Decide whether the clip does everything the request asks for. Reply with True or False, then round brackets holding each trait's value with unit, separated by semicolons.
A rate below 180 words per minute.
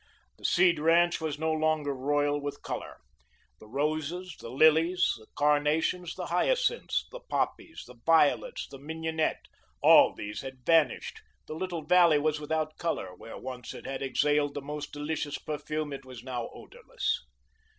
True (155 wpm)